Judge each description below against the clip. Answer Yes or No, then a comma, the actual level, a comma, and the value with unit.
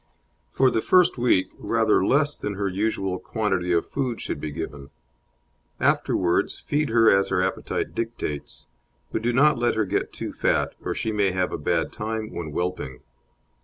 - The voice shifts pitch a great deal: No, average, 4.3 semitones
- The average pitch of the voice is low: Yes, low, 105 Hz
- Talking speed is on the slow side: No, average, 165 wpm